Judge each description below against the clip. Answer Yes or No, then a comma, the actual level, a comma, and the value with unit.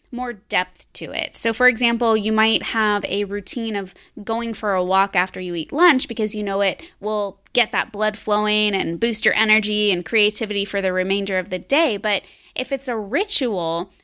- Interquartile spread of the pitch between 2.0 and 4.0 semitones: Yes, average, 3.1 semitones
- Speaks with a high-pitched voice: Yes, high, 210 Hz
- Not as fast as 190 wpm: No, average, 200 wpm